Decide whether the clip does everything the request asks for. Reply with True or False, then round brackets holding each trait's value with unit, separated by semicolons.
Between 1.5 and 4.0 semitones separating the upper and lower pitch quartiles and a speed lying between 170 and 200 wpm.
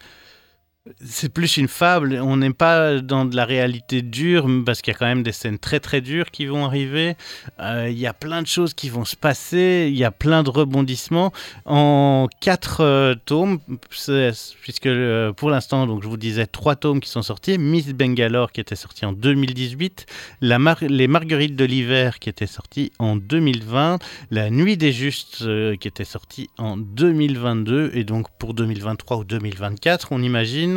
False (4.5 semitones; 185 wpm)